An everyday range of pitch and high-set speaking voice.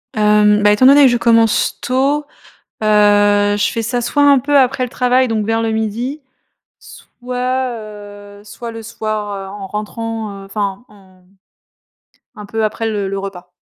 Yes: average, 3.0 semitones; high, 215 Hz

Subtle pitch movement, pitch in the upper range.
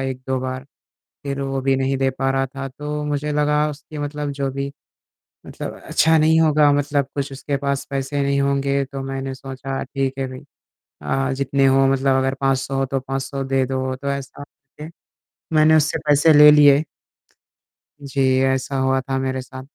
No: narrow, 1.4 semitones; low, 135 Hz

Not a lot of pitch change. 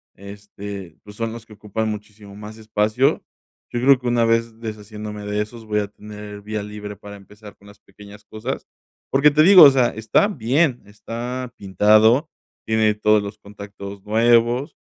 Yes: narrow, 2.3 semitones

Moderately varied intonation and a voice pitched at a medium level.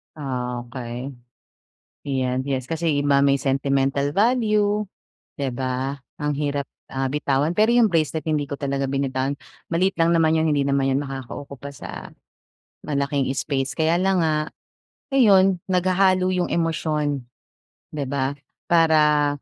Yes: average, 3.4 semitones; medium, 145 Hz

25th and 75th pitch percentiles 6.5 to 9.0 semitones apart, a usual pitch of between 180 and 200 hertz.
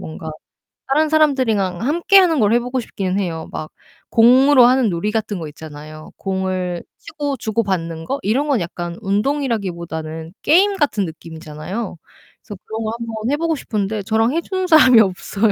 No: wide, 7.3 semitones; high, 215 Hz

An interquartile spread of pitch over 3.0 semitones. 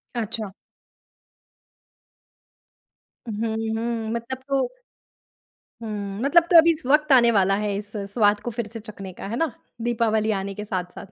No: narrow, 2.5 semitones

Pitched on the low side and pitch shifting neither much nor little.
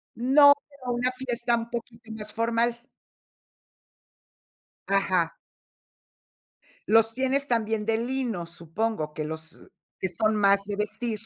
No: high, 225 Hz; average, 3.3 semitones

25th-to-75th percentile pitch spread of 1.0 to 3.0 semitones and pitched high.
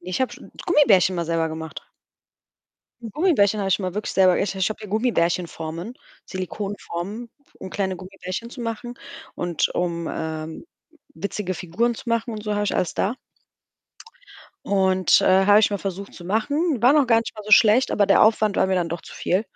No: average, 3.6 semitones; high, 200 Hz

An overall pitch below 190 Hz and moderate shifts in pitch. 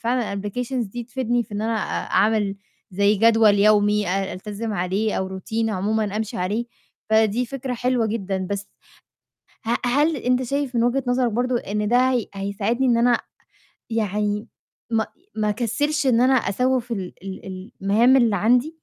No: high, 225 Hz; average, 3.3 semitones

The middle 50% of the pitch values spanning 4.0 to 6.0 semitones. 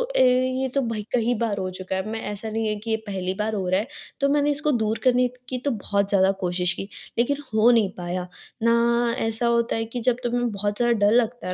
No: average, 3.2 semitones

